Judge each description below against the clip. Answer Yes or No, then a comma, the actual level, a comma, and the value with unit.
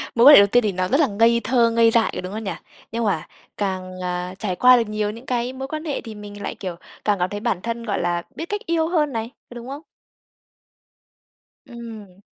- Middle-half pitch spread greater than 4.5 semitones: No, average, 3.8 semitones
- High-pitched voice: Yes, high, 225 Hz